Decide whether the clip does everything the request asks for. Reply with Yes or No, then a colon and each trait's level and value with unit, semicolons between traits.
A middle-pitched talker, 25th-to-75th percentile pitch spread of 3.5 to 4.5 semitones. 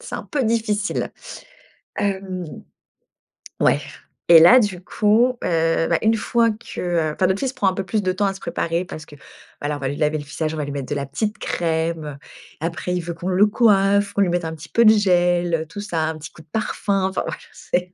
Yes: medium, 180 Hz; average, 4.1 semitones